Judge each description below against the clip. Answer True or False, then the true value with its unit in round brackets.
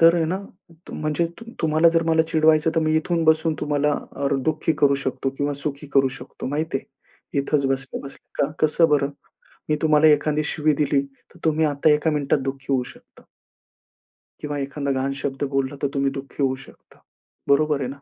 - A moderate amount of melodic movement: False (2.3 semitones)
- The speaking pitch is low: False (150 Hz)